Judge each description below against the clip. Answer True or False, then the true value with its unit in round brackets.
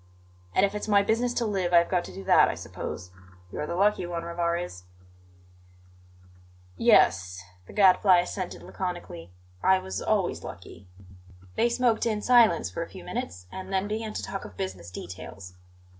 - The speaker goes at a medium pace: True (170 wpm)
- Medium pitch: True (180 Hz)